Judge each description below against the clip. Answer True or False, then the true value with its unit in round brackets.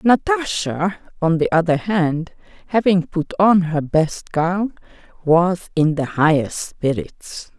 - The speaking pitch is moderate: True (175 Hz)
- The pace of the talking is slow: True (125 wpm)